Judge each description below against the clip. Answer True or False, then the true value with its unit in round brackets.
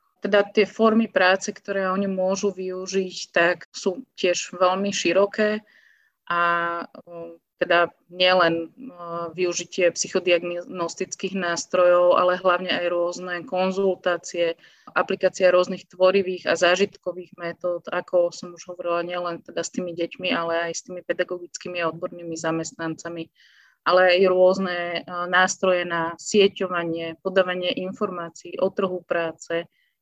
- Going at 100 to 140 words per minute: True (115 wpm)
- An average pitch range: False (1.6 semitones)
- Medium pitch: True (180 Hz)